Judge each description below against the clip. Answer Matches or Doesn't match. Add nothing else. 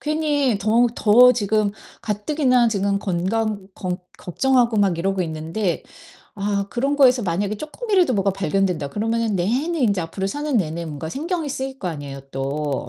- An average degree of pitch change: Doesn't match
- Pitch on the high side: Matches